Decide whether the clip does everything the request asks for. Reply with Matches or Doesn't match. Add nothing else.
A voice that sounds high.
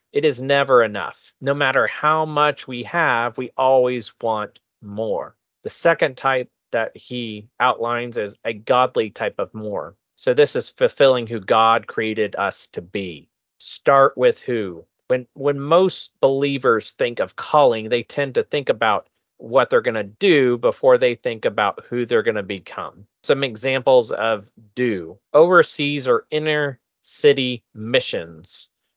Doesn't match